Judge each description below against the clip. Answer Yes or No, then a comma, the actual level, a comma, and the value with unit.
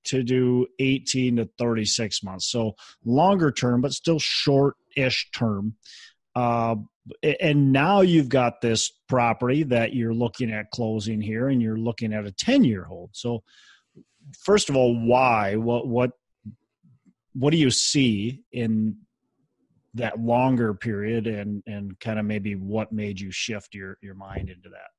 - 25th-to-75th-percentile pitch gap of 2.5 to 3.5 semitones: Yes, average, 3.1 semitones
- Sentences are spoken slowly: No, average, 150 wpm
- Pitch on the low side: Yes, low, 115 Hz